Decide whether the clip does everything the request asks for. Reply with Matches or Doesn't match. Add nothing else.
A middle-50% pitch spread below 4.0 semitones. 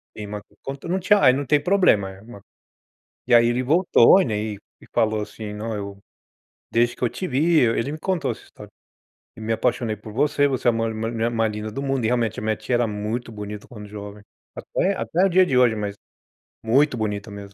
Doesn't match